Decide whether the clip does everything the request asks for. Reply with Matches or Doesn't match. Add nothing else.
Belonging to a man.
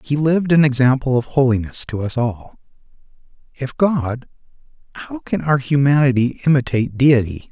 Matches